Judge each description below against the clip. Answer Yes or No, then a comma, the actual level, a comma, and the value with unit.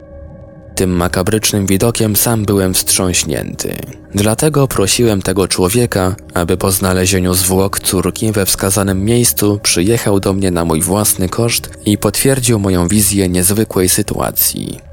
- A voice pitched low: Yes, low, 100 Hz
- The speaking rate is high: No, average, 125 wpm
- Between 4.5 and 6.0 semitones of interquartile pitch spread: No, average, 2.8 semitones